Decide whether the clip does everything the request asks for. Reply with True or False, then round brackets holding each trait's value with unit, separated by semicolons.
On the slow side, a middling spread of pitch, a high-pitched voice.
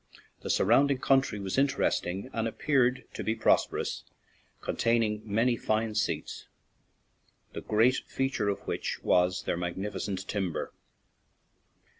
False (120 wpm; 4.2 semitones; 110 Hz)